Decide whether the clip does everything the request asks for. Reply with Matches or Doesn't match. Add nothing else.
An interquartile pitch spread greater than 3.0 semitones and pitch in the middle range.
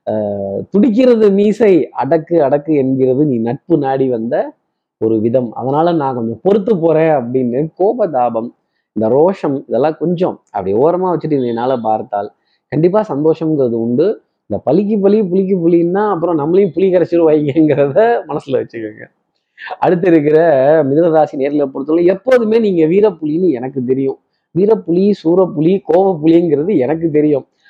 Matches